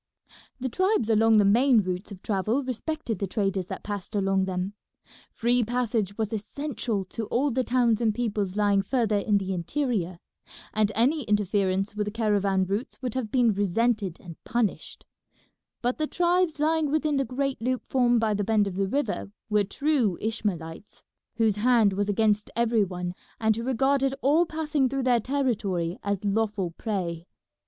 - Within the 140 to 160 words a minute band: No, average, 170 wpm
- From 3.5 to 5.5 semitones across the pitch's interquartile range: Yes, average, 4.2 semitones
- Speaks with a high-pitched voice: Yes, high, 220 Hz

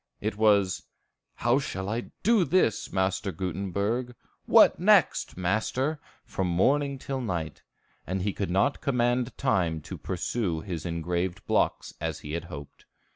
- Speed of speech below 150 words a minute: Yes, average, 140 wpm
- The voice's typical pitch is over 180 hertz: No, low, 100 Hz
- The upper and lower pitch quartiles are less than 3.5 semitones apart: No, wide, 5.6 semitones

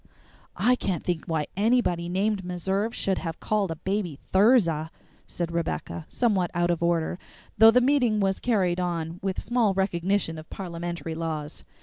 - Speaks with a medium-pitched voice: Yes, medium, 180 Hz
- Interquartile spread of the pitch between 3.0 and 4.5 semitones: Yes, average, 3.5 semitones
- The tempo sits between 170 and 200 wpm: No, average, 155 wpm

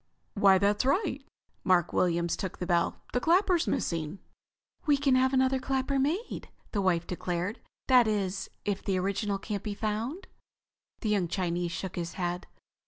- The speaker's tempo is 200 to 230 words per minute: No, average, 160 wpm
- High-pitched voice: Yes, high, 200 Hz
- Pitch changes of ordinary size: No, wide, 6.4 semitones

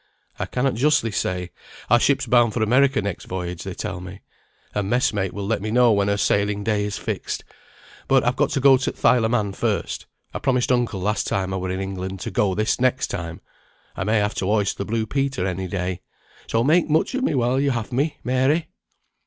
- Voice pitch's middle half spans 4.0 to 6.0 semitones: Yes, average, 4.8 semitones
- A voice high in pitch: No, low, 110 Hz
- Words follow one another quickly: Yes, fast, 225 wpm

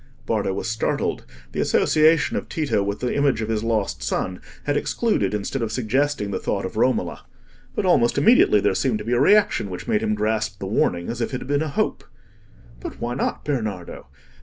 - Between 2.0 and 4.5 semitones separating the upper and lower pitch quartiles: No, average, 5.2 semitones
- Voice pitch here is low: Yes, low, 115 Hz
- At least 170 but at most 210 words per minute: Yes, fast, 205 wpm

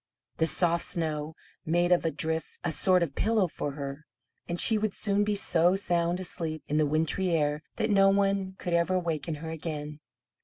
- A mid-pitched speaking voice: Yes, medium, 170 Hz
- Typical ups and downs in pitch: Yes, average, 3.2 semitones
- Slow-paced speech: No, average, 190 wpm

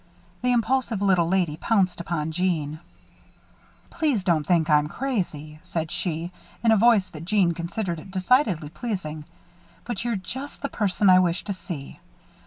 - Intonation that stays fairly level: No, average, 5.2 semitones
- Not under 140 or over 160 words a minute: Yes, average, 155 wpm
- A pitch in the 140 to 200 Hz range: Yes, medium, 185 Hz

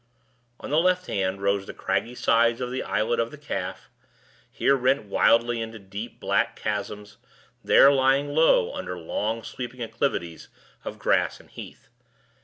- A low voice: Yes, low, 115 Hz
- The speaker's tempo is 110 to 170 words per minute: Yes, average, 155 wpm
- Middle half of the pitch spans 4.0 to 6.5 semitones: Yes, average, 4.7 semitones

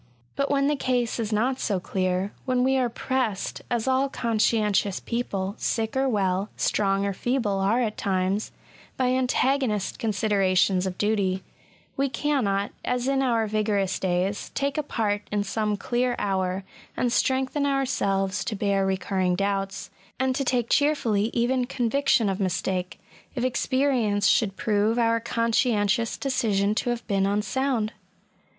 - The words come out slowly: No, average, 145 wpm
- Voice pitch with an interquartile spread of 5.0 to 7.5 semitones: No, average, 4.3 semitones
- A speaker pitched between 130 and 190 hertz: No, high, 220 Hz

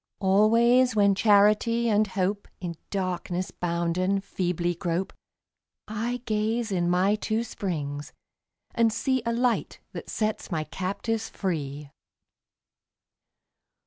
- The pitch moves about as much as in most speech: Yes, average, 4.1 semitones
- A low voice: No, high, 200 Hz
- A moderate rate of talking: No, slow, 110 wpm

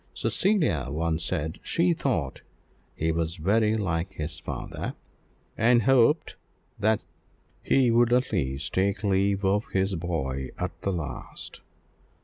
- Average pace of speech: No, slow, 130 wpm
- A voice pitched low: Yes, very low, 95 Hz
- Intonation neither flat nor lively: No, wide, 5.9 semitones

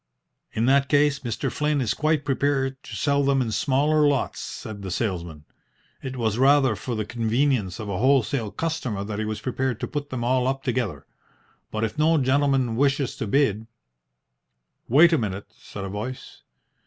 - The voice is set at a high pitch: No, low, 130 Hz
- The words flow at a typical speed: Yes, average, 180 wpm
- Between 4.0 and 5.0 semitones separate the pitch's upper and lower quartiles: Yes, average, 4.5 semitones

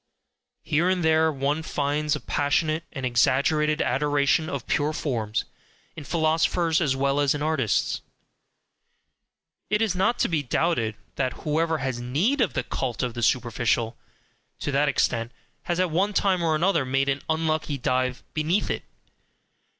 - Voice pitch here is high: No, medium, 150 Hz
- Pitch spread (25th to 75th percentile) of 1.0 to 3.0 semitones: No, average, 3.6 semitones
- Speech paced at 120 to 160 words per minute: Yes, average, 155 wpm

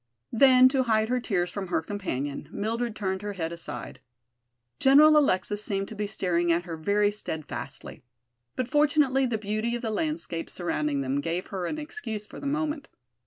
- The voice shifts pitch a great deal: Yes, wide, 6.6 semitones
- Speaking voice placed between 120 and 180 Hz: No, high, 210 Hz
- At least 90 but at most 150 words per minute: No, average, 175 wpm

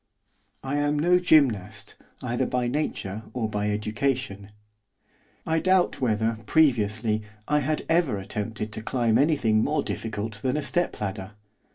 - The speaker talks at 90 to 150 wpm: Yes, average, 140 wpm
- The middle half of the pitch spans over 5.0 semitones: Yes, wide, 5.6 semitones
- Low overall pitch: Yes, low, 115 Hz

